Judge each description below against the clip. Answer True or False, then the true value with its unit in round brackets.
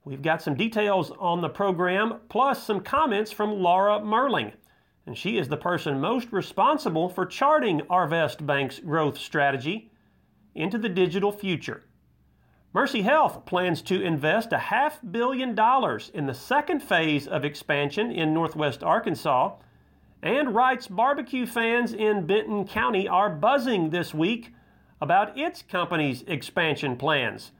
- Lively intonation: True (6.2 semitones)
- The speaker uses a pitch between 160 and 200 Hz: True (185 Hz)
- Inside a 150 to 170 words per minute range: False (140 wpm)